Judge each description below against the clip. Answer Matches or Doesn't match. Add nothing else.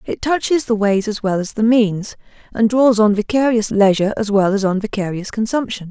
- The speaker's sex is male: Doesn't match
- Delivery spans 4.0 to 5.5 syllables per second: Matches